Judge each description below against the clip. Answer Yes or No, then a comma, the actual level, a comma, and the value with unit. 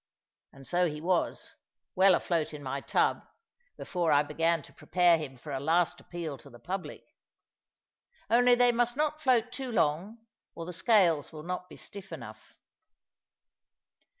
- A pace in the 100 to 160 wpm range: Yes, average, 155 wpm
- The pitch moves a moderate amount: No, wide, 6.1 semitones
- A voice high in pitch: No, medium, 175 Hz